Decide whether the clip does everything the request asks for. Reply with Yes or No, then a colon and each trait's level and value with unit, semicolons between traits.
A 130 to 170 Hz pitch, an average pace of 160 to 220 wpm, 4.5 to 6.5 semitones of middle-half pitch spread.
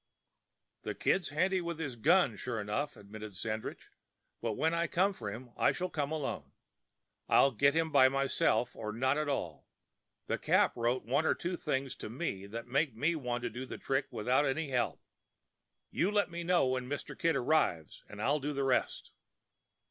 Yes: low, 135 Hz; average, 185 wpm; average, 5.2 semitones